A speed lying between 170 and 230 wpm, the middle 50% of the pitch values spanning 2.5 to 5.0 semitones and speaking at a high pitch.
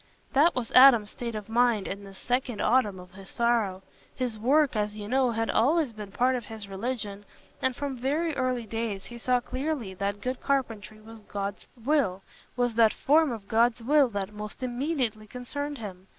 Yes: average, 180 wpm; average, 3.7 semitones; high, 235 Hz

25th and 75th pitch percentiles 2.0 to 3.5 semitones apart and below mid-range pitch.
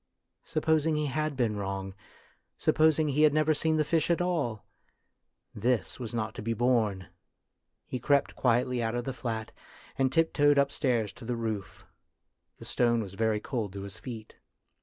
No: average, 4.9 semitones; low, 125 Hz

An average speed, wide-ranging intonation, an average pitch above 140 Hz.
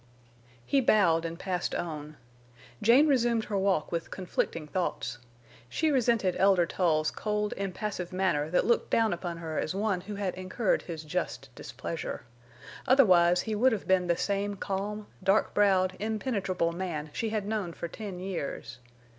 No: average, 155 wpm; average, 3.8 semitones; high, 190 Hz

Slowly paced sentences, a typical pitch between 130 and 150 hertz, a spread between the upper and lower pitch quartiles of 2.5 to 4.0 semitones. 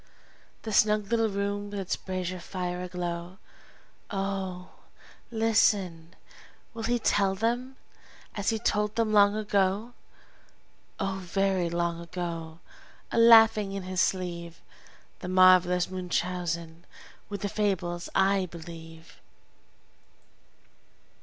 No: slow, 105 wpm; high, 190 Hz; average, 2.9 semitones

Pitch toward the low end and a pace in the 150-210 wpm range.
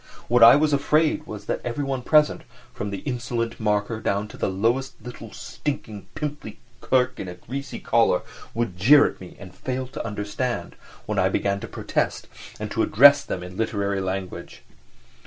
Yes: low, 115 Hz; average, 175 wpm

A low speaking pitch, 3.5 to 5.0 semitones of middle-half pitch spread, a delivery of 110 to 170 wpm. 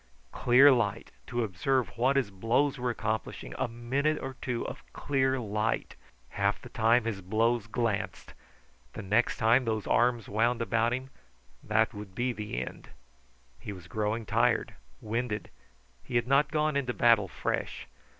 No: low, 115 Hz; average, 2.8 semitones; average, 155 wpm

